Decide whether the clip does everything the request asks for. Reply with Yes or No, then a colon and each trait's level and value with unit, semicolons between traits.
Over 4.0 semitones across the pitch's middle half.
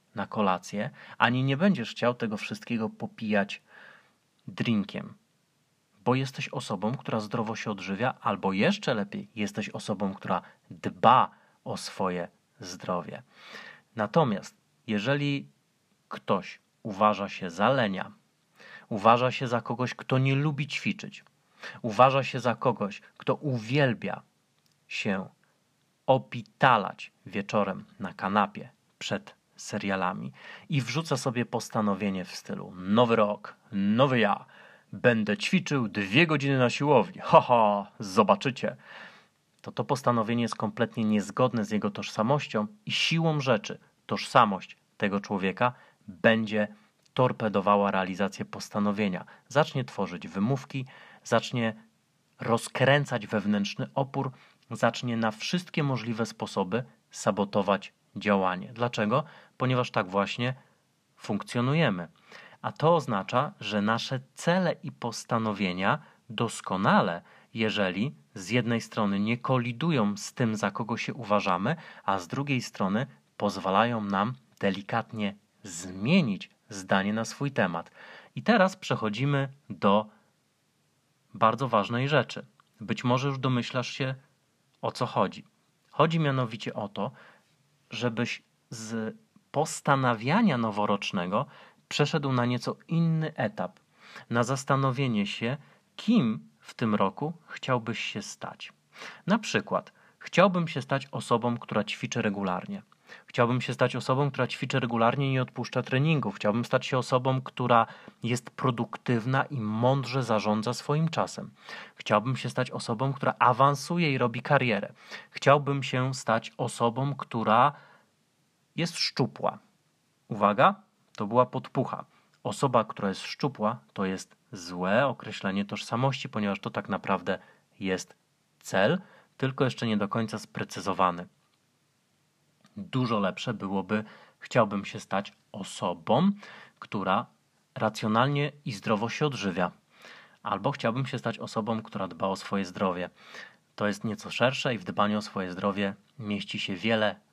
Yes: average, 4.4 semitones